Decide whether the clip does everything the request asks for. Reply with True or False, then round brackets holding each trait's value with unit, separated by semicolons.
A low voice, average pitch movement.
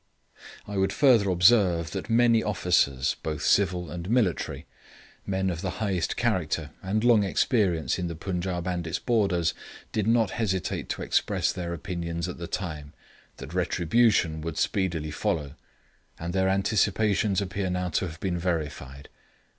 True (90 Hz; 3.2 semitones)